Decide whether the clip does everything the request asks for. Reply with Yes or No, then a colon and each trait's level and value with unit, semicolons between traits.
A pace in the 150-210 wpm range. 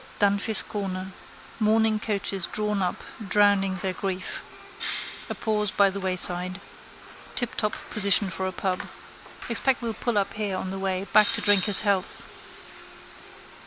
No: average, 140 wpm